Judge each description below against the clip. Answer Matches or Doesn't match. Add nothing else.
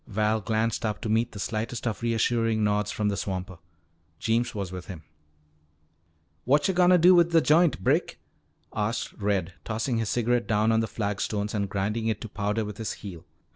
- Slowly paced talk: Doesn't match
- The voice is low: Matches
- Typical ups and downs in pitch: Doesn't match